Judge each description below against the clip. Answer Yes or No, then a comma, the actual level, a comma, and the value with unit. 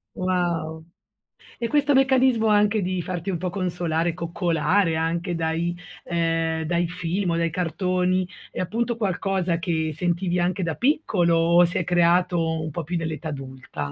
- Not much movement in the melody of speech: Yes, narrow, 2.1 semitones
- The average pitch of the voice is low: No, medium, 175 Hz